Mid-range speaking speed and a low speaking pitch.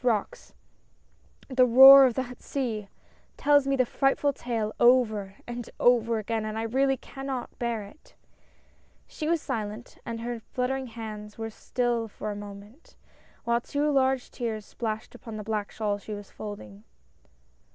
No: average, 170 wpm; high, 235 Hz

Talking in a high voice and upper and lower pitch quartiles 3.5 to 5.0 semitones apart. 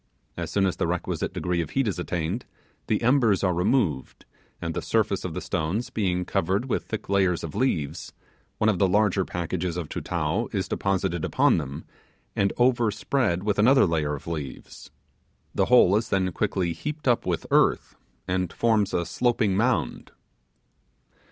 No: very low, 95 Hz; average, 4.3 semitones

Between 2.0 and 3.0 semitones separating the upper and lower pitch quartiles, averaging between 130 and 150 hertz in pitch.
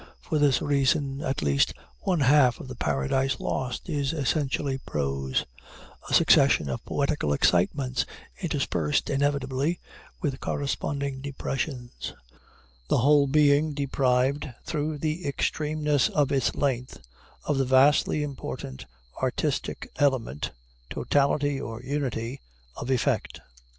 Yes: narrow, 2.4 semitones; medium, 140 Hz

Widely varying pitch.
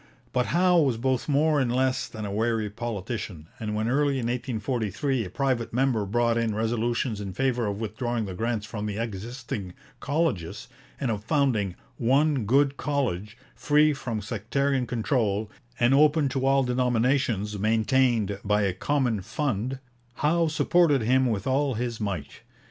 No: average, 4.0 semitones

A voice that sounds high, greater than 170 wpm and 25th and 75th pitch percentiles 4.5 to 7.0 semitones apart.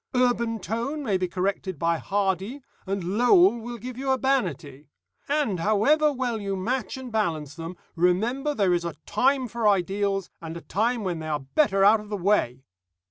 Yes: high, 205 Hz; average, 180 wpm; wide, 5.6 semitones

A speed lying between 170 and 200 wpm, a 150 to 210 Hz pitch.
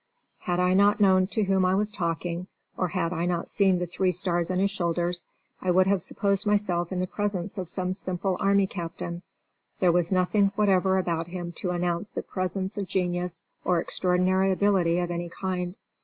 Yes: average, 190 wpm; medium, 185 Hz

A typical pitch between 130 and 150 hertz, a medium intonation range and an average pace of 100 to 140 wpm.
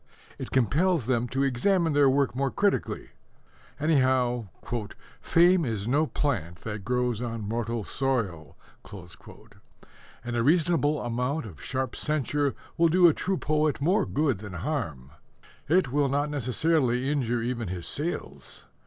Yes: low, 135 Hz; average, 4.5 semitones; slow, 135 wpm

